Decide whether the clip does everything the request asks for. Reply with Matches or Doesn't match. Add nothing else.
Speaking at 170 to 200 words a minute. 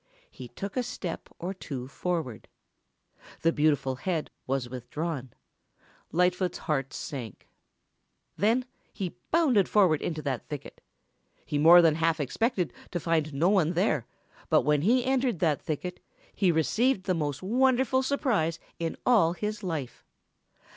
Doesn't match